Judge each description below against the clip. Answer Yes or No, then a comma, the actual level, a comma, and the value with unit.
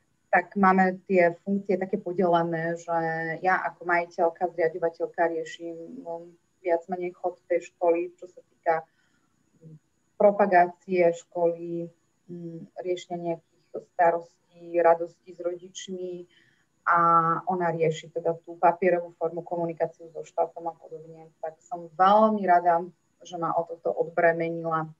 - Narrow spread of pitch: Yes, narrow, 1.2 semitones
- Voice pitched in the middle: Yes, medium, 170 Hz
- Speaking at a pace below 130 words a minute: Yes, average, 120 wpm